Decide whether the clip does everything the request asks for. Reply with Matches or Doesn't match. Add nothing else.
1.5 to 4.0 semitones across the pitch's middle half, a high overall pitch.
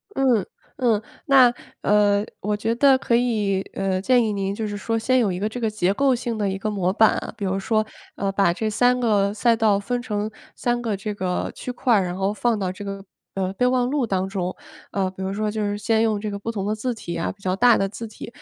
Matches